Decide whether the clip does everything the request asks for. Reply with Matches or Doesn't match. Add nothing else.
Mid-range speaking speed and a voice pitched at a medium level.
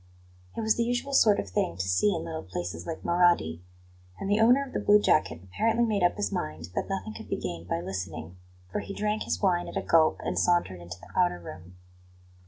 Doesn't match